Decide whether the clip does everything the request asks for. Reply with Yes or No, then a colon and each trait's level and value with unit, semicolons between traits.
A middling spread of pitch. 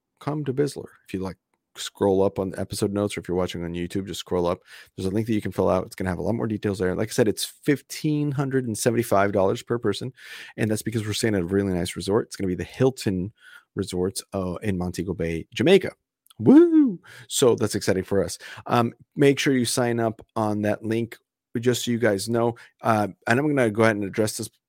Yes: average, 4.0 semitones